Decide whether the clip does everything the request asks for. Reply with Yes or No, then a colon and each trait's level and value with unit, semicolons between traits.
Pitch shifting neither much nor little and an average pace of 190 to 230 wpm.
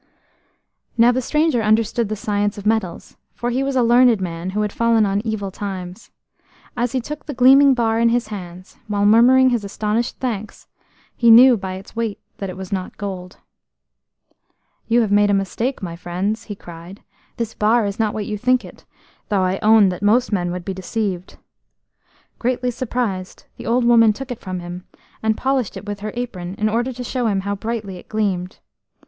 Yes: average, 3.6 semitones; average, 195 wpm